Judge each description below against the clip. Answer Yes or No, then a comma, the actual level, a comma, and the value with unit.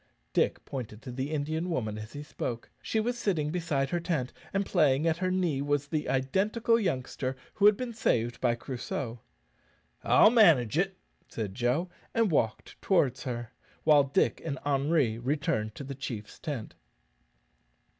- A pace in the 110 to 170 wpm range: Yes, average, 160 wpm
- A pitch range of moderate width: No, wide, 5.8 semitones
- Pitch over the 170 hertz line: No, medium, 145 Hz